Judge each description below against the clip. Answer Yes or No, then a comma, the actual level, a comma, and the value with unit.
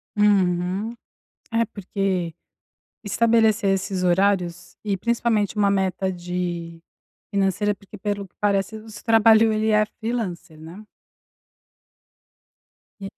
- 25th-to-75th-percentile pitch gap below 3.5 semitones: Yes, average, 2.9 semitones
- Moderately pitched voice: No, high, 200 Hz